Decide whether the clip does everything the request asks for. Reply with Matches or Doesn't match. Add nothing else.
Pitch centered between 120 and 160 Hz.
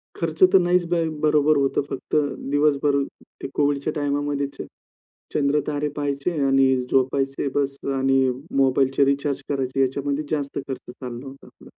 Matches